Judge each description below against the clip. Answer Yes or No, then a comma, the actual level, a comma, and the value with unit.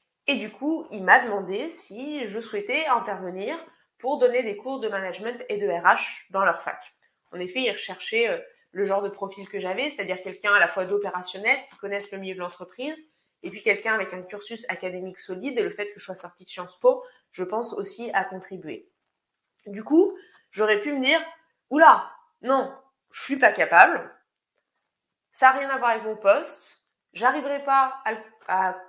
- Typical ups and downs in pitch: No, wide, 6.6 semitones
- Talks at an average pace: Yes, average, 190 wpm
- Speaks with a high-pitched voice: Yes, high, 220 Hz